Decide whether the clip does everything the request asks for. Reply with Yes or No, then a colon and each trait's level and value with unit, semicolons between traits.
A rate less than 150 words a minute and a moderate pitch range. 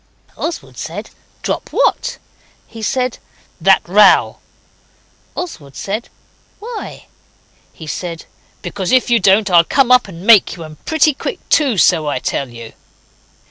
No: average, 140 wpm; wide, 7.5 semitones